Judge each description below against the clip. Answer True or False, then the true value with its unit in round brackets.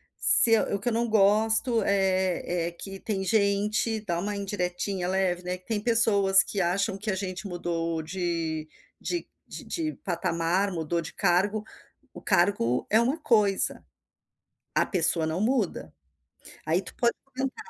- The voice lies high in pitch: True (195 Hz)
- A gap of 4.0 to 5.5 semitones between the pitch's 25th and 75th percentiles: False (3.5 semitones)